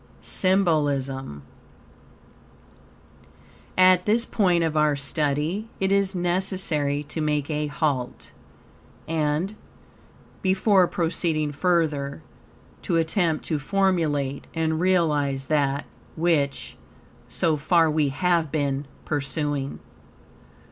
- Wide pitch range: No, average, 3.7 semitones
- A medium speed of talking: No, slow, 95 wpm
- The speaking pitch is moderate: Yes, medium, 155 Hz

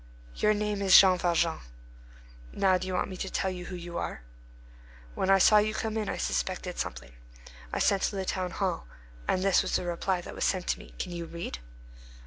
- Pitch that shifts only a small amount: Yes, narrow, 2.1 semitones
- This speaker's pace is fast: Yes, fast, 215 wpm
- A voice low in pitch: No, medium, 185 Hz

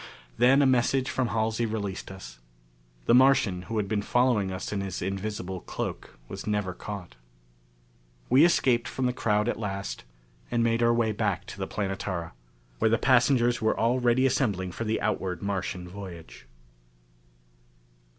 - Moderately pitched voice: No, low, 110 Hz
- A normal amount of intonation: Yes, average, 3.9 semitones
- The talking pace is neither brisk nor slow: Yes, average, 155 wpm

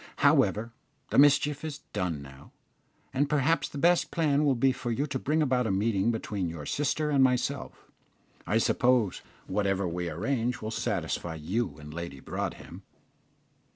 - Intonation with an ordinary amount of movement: No, wide, 7.5 semitones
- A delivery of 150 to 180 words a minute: Yes, average, 155 wpm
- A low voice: Yes, low, 115 Hz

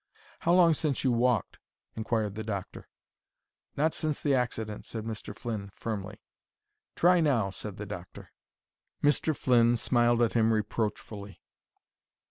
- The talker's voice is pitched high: No, low, 115 Hz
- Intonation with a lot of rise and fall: No, average, 3.8 semitones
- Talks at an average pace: No, slow, 130 wpm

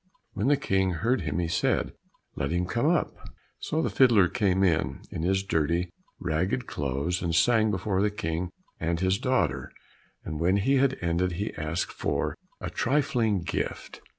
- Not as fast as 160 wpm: No, average, 170 wpm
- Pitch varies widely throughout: No, average, 5.0 semitones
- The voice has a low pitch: Yes, very low, 95 Hz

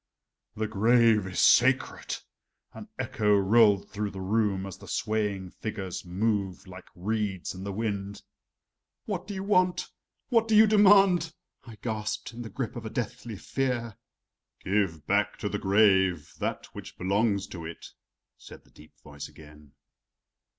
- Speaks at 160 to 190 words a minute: No, average, 150 wpm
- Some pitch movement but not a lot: Yes, average, 3.5 semitones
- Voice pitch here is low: Yes, low, 105 Hz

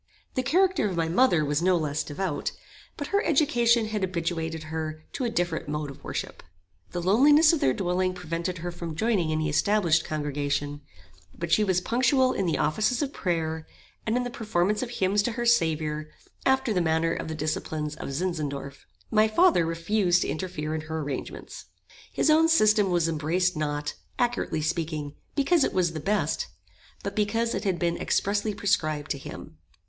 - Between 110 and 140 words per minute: No, average, 180 wpm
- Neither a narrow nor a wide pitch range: No, wide, 5.7 semitones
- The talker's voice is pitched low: No, medium, 175 Hz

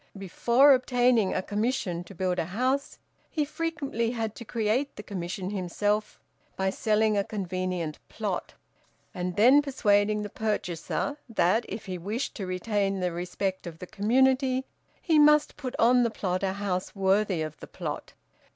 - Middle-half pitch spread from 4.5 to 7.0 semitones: Yes, average, 5.0 semitones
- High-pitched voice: Yes, high, 210 Hz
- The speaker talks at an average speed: Yes, average, 160 wpm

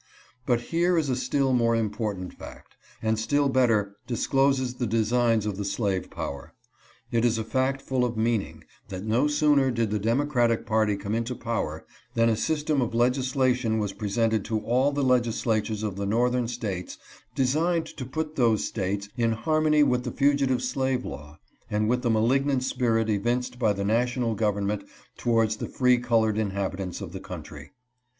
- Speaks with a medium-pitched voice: No, low, 115 Hz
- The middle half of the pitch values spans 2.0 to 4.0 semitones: Yes, average, 3.3 semitones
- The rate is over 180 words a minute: No, average, 170 wpm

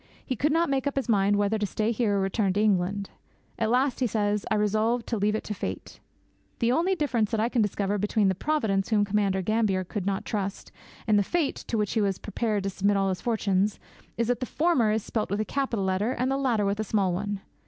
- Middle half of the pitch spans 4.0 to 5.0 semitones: No, average, 3.0 semitones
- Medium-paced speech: No, fast, 245 wpm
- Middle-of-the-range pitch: No, high, 210 Hz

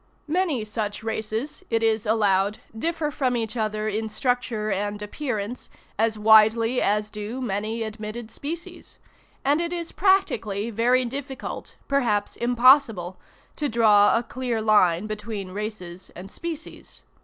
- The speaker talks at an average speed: No, slow, 130 wpm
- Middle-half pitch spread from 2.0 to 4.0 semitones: Yes, average, 3.3 semitones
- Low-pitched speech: No, high, 220 Hz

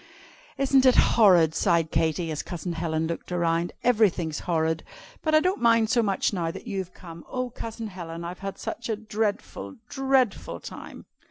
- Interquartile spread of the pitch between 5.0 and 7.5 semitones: Yes, wide, 5.5 semitones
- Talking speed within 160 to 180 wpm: Yes, average, 170 wpm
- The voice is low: No, high, 190 Hz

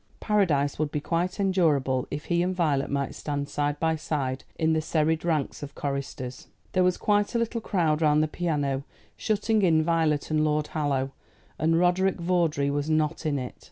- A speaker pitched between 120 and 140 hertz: No, medium, 155 Hz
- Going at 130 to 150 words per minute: No, average, 185 wpm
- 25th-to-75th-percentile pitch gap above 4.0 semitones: No, average, 3.4 semitones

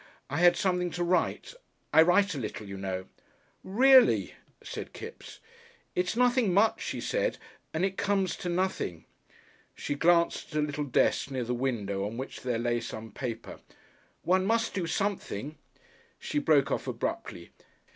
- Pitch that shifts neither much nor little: No, wide, 8.0 semitones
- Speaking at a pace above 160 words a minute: No, average, 155 wpm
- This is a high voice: No, medium, 170 Hz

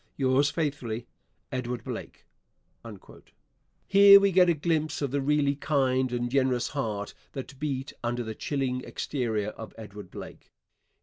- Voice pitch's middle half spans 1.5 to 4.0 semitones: Yes, average, 3.3 semitones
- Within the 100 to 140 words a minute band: Yes, slow, 135 wpm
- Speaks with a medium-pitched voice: No, low, 130 Hz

